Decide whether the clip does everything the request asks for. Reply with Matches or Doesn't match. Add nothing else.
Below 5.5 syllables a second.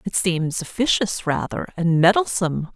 Matches